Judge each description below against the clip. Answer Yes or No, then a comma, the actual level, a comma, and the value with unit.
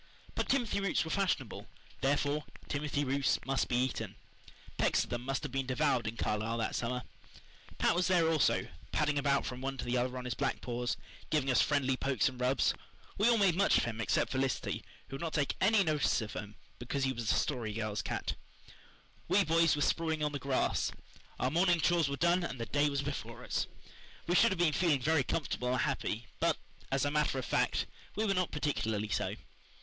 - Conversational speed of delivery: No, fast, 210 wpm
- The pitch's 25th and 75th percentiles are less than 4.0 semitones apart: No, average, 4.3 semitones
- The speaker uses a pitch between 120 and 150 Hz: Yes, medium, 140 Hz